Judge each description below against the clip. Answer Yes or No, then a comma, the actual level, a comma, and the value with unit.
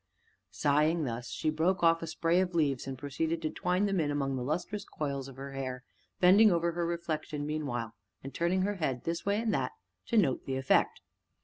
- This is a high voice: No, medium, 155 Hz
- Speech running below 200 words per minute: No, fast, 205 wpm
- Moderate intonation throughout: Yes, average, 4.2 semitones